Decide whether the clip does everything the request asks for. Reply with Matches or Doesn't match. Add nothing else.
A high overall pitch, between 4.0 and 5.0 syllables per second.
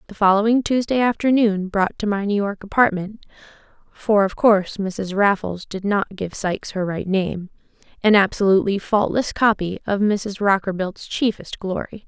Matches